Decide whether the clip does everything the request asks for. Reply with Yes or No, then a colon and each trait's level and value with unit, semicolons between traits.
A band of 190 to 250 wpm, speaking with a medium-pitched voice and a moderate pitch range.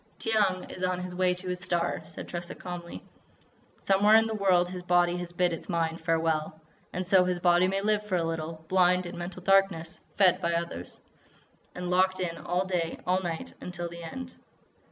No: average, 195 wpm; medium, 180 Hz; narrow, 1.5 semitones